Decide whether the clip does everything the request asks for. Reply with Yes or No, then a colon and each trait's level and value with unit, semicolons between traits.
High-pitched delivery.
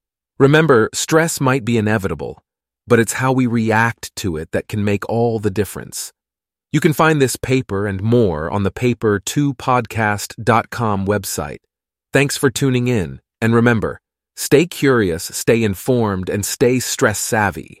No: low, 115 Hz